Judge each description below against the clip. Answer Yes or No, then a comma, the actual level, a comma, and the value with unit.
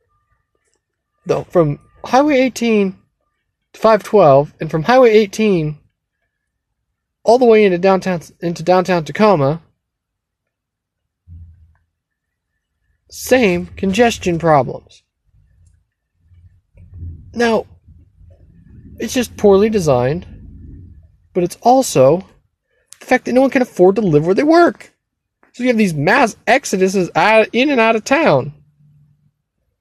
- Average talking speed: No, slow, 105 wpm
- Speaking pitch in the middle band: Yes, medium, 160 Hz